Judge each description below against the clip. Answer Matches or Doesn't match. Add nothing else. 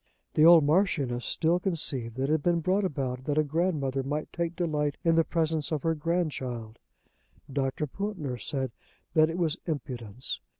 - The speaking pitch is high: Doesn't match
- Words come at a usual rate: Matches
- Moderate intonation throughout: Matches